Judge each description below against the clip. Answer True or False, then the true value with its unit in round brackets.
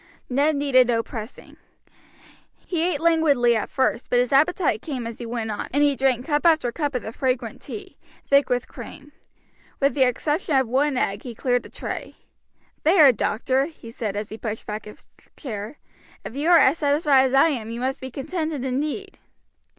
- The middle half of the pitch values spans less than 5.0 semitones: True (3.8 semitones)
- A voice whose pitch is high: True (265 Hz)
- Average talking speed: True (190 wpm)